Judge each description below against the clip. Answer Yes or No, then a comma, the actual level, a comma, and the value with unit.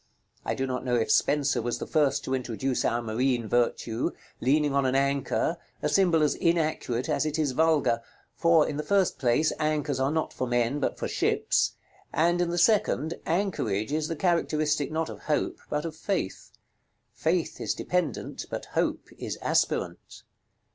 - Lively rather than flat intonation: No, average, 4.0 semitones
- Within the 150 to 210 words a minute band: Yes, average, 175 wpm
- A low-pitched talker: No, medium, 150 Hz